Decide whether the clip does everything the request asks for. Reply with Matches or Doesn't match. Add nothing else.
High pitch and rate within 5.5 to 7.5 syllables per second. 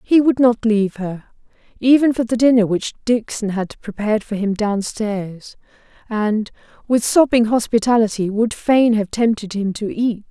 Doesn't match